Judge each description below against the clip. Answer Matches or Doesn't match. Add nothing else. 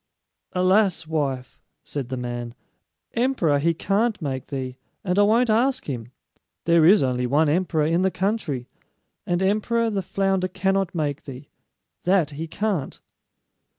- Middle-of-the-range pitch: Matches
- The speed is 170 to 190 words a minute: Doesn't match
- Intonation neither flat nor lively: Doesn't match